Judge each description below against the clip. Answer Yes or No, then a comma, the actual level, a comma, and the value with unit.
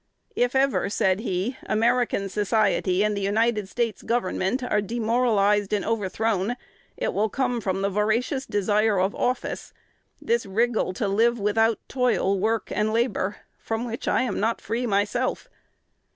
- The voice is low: No, high, 220 Hz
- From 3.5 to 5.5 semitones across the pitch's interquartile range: No, average, 3.0 semitones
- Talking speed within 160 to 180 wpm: No, average, 150 wpm